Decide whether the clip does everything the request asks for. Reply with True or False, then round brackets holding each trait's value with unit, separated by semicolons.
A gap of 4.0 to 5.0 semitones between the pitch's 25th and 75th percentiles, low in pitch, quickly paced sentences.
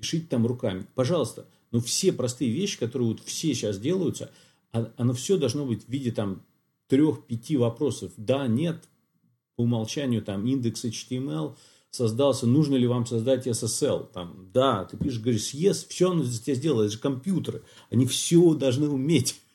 True (4.3 semitones; 125 Hz; 165 wpm)